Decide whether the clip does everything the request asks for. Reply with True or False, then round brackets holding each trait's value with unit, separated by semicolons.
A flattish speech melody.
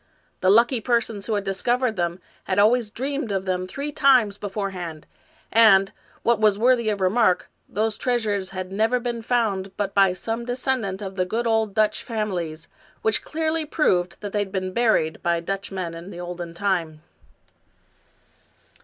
False (3.8 semitones)